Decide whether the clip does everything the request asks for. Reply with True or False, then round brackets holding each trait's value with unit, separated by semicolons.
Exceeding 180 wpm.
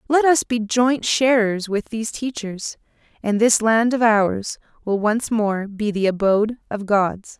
False (170 wpm)